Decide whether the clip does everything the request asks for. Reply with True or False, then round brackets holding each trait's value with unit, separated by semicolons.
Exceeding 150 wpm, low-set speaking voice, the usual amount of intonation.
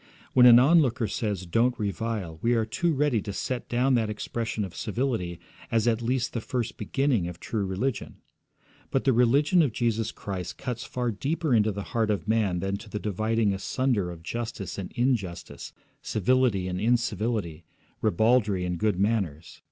True (170 wpm; 115 Hz; 3.9 semitones)